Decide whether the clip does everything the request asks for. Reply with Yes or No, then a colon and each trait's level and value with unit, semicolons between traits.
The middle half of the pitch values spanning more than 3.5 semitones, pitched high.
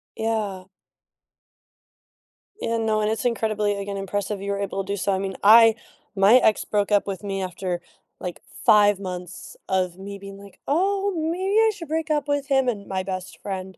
No: average, 3.1 semitones; high, 205 Hz